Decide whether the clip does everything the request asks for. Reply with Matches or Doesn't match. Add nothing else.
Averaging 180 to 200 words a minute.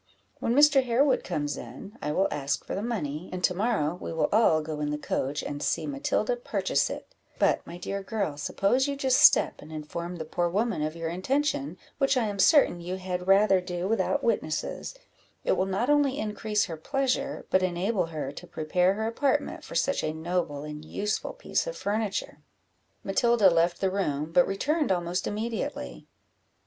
Matches